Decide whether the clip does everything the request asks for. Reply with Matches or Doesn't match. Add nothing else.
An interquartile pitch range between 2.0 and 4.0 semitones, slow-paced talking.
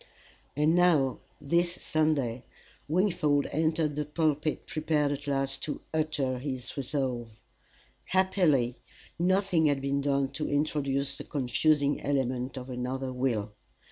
Matches